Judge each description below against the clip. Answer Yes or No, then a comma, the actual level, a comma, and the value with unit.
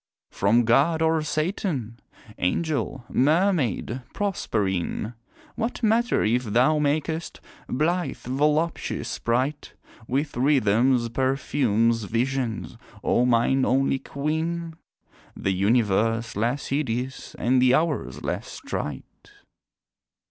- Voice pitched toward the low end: Yes, low, 130 Hz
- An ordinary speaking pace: No, slow, 95 wpm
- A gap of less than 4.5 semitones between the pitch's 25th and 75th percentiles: No, average, 4.8 semitones